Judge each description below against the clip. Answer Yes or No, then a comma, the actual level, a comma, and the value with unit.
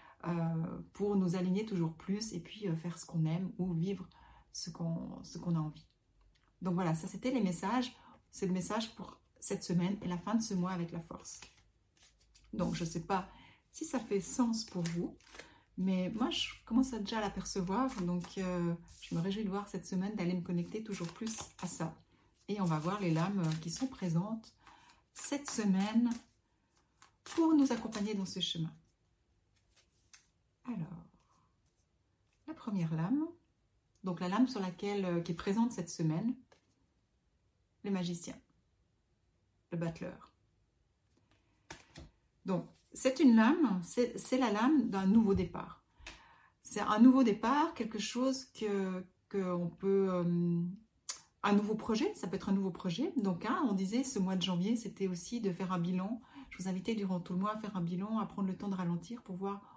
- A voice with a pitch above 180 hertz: Yes, high, 190 Hz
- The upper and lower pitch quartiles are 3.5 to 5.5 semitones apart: Yes, average, 3.9 semitones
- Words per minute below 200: Yes, average, 175 wpm